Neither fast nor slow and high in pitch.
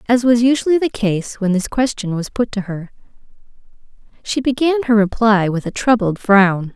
Yes: average, 180 wpm; high, 220 Hz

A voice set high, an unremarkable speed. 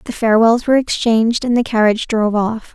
Yes: high, 225 Hz; average, 195 wpm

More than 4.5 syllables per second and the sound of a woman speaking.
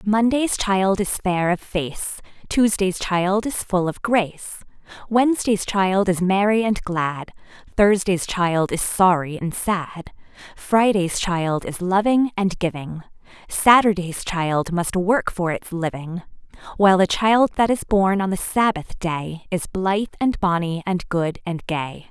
No: 4.0 syllables/s; female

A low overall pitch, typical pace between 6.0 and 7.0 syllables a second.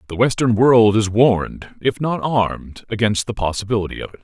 No: low, 110 Hz; 5.5 syllables/s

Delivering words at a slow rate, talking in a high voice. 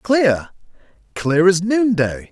No: slow, 80 wpm; medium, 180 Hz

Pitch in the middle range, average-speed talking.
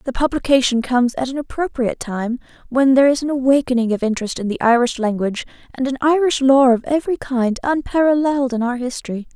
No: very high, 260 Hz; average, 185 wpm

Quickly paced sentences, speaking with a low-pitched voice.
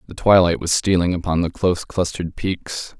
No: average, 180 wpm; very low, 90 Hz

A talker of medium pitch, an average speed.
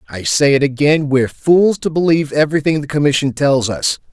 Yes: medium, 145 Hz; average, 190 wpm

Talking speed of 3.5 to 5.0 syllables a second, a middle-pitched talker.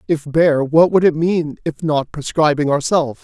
Yes: 4.7 syllables/s; medium, 155 Hz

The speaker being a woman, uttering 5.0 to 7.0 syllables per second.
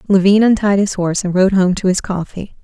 Yes: female; 5.8 syllables/s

